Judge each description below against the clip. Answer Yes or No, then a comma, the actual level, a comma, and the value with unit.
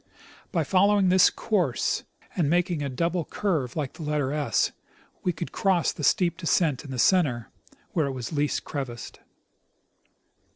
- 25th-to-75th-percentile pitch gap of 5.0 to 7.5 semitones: No, average, 4.5 semitones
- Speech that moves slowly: No, average, 155 wpm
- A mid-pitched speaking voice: Yes, medium, 155 Hz